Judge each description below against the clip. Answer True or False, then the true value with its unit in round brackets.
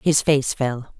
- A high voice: False (135 Hz)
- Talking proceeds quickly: False (180 wpm)